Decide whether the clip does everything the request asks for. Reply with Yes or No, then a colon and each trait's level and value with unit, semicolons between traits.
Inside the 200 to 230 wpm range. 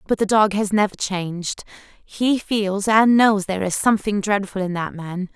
No: average, 190 wpm